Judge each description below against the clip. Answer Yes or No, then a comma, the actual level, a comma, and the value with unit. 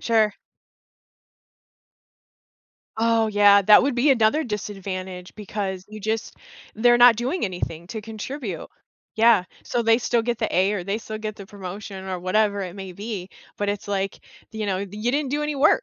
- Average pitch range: Yes, average, 3.0 semitones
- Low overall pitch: No, high, 210 Hz